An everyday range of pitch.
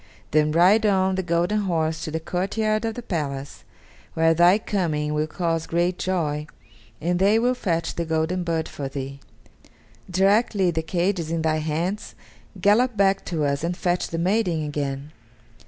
Yes: average, 3.5 semitones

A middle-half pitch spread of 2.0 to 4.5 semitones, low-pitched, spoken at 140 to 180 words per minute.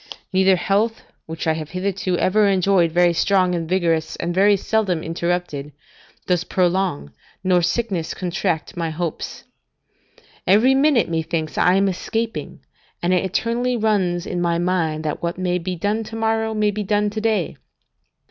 No: average, 3.4 semitones; medium, 185 Hz; average, 155 wpm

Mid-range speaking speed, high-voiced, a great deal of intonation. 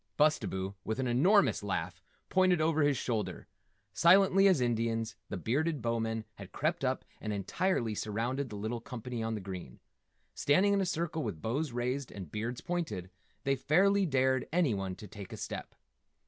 No: average, 165 wpm; low, 120 Hz; wide, 6.6 semitones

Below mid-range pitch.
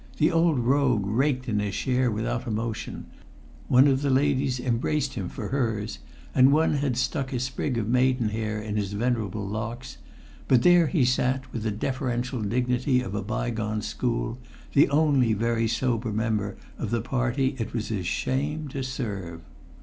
Yes: low, 125 Hz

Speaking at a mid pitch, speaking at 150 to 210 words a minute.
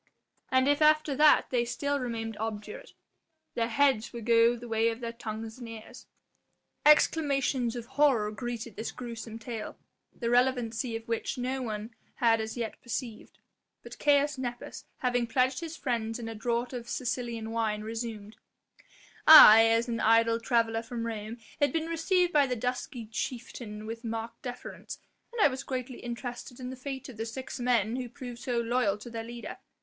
No: high, 235 Hz; average, 175 wpm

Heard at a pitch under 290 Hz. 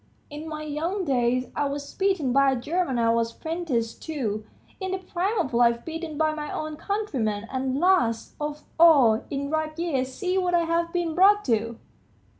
No: very high, 300 Hz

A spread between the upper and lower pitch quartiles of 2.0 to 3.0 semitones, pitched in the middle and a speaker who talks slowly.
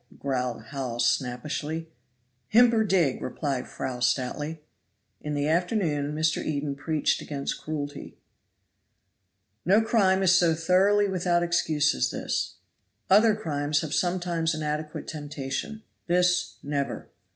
No: average, 3.9 semitones; medium, 155 Hz; slow, 120 wpm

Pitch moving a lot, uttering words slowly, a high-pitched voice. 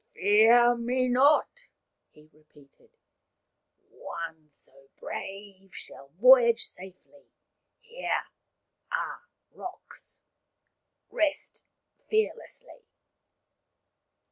Yes: wide, 7.2 semitones; slow, 75 wpm; high, 235 Hz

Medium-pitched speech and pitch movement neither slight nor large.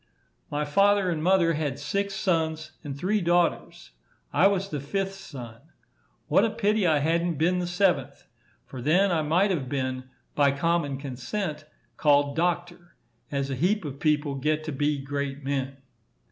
Yes: medium, 155 Hz; average, 4.2 semitones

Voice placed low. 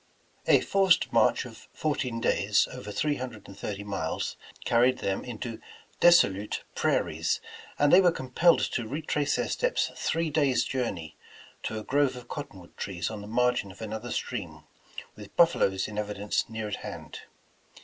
Yes: low, 115 Hz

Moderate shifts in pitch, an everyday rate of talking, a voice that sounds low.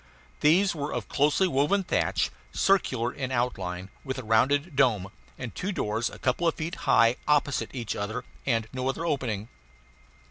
Yes: average, 4.8 semitones; average, 165 wpm; low, 130 Hz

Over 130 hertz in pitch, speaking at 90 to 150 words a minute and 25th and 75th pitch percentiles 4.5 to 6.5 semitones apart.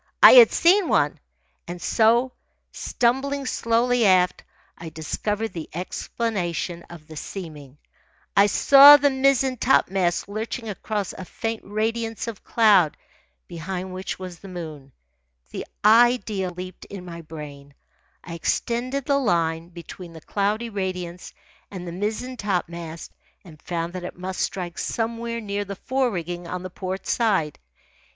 Yes: high, 190 Hz; average, 140 wpm; average, 5.0 semitones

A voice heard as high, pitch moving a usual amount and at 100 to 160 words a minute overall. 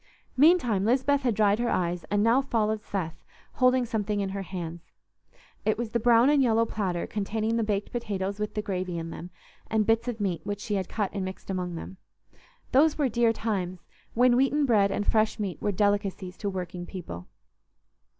No: high, 210 Hz; average, 3.5 semitones; average, 190 wpm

